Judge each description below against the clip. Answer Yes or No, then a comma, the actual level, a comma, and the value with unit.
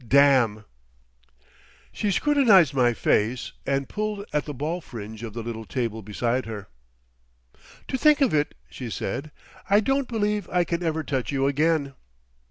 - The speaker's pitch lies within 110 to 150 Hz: Yes, medium, 140 Hz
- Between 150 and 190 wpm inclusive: Yes, average, 155 wpm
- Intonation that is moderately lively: No, wide, 8.6 semitones